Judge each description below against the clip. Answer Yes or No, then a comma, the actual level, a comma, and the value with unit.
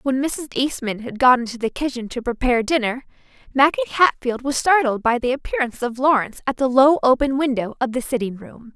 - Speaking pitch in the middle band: No, very high, 260 Hz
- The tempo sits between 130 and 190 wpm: No, average, 200 wpm